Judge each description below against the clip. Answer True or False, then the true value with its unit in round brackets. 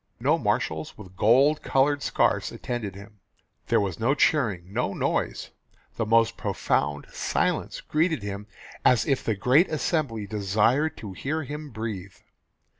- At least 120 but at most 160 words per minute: True (140 wpm)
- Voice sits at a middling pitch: False (115 Hz)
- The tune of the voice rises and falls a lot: True (6.1 semitones)